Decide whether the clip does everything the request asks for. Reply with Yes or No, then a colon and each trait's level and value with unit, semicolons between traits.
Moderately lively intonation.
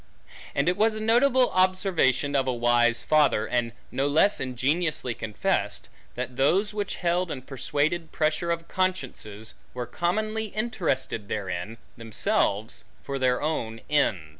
No: wide, 7.3 semitones